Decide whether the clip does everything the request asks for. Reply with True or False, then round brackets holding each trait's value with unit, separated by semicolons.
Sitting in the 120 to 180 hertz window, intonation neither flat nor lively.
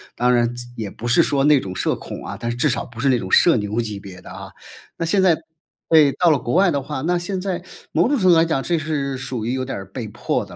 False (135 Hz; 5.8 semitones)